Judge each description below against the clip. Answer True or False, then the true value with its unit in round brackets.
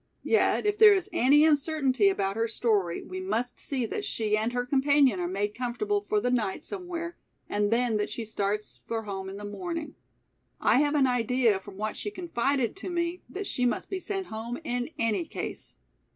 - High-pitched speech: True (245 Hz)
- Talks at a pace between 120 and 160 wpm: False (195 wpm)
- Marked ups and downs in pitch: True (7.5 semitones)